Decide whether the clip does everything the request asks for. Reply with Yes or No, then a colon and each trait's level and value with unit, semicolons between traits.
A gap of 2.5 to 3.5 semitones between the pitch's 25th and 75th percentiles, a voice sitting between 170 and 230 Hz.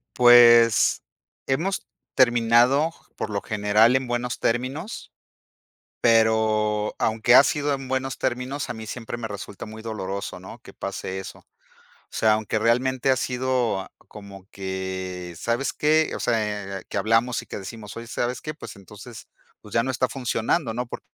No: average, 3.2 semitones; low, 115 Hz